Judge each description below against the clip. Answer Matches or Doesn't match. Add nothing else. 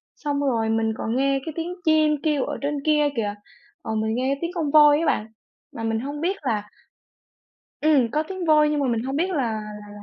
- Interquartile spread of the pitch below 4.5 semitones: Doesn't match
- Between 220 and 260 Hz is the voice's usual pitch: Doesn't match